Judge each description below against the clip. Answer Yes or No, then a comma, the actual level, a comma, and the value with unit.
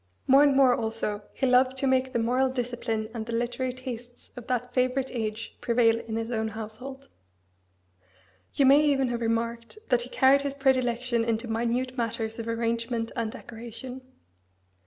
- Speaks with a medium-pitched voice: No, high, 240 Hz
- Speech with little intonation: Yes, narrow, 2.2 semitones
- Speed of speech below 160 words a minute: No, average, 165 wpm